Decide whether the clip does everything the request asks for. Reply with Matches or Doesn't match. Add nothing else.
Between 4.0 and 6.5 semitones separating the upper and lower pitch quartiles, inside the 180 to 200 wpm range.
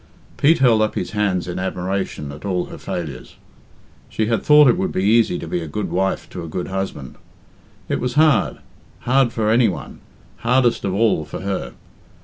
Matches